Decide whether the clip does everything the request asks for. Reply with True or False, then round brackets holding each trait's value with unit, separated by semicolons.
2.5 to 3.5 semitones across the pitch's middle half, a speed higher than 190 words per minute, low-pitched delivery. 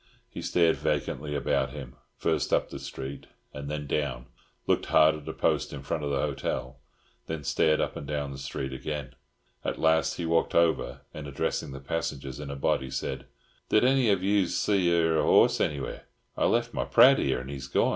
True (3.1 semitones; 200 wpm; 75 Hz)